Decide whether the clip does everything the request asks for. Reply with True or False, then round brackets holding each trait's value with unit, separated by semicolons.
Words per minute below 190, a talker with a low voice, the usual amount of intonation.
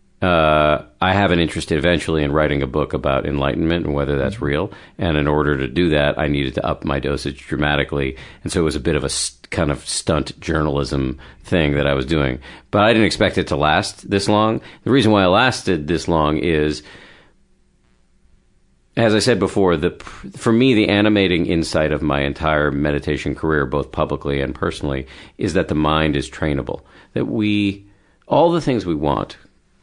False (195 wpm; 75 Hz; 4.1 semitones)